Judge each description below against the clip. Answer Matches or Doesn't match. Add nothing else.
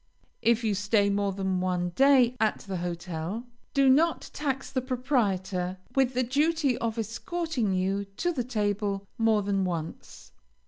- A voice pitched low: Doesn't match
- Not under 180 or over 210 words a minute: Doesn't match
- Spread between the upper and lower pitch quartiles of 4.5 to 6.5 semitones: Matches